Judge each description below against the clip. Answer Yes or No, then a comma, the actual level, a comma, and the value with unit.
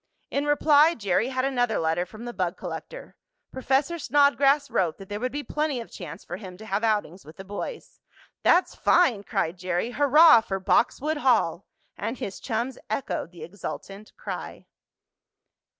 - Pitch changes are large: Yes, wide, 6.8 semitones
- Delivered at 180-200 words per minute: No, average, 165 wpm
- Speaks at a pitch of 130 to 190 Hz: No, high, 230 Hz